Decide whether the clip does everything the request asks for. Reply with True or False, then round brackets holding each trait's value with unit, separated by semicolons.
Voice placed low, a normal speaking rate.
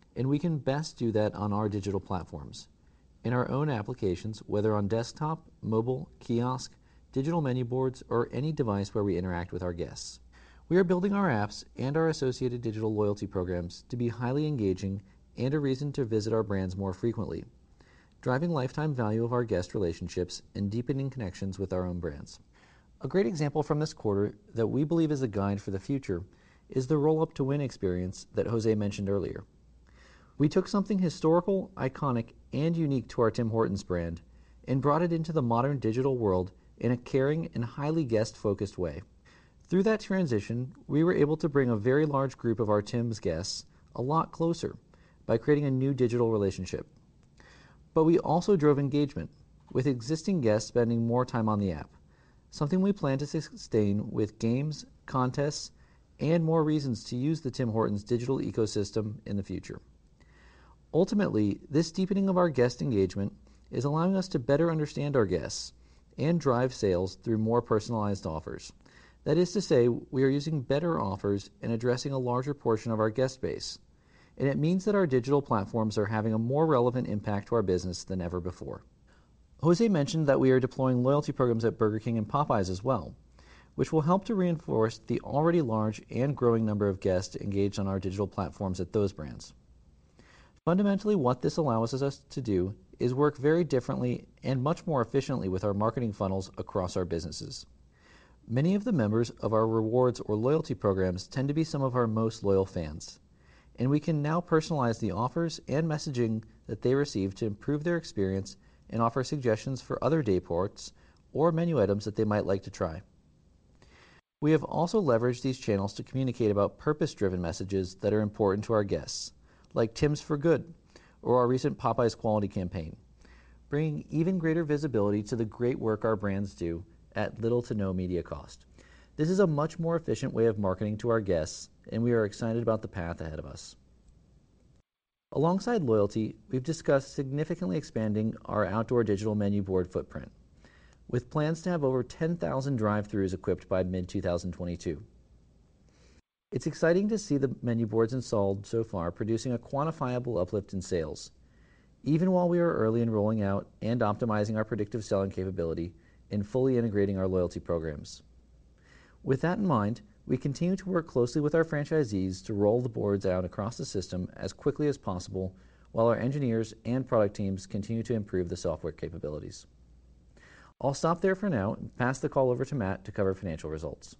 True (115 Hz; 180 wpm)